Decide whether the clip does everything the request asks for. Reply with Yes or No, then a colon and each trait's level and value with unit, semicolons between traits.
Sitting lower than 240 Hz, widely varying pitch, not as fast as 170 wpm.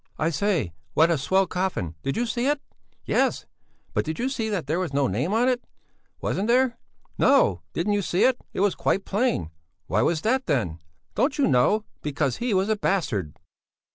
No: high, 190 Hz; wide, 8.1 semitones; average, 195 wpm